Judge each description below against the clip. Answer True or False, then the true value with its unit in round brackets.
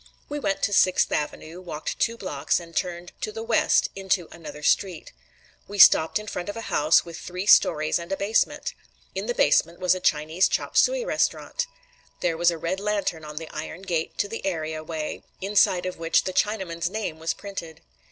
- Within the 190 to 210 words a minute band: True (195 wpm)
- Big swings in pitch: False (3.7 semitones)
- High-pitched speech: False (180 Hz)